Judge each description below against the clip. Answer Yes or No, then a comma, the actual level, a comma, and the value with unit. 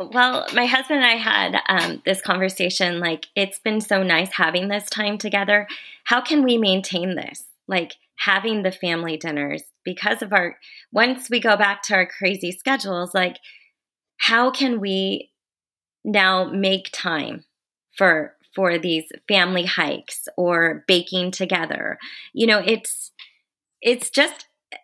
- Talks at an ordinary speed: Yes, average, 145 wpm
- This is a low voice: No, high, 195 Hz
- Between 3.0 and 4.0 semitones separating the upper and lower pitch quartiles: No, average, 4.7 semitones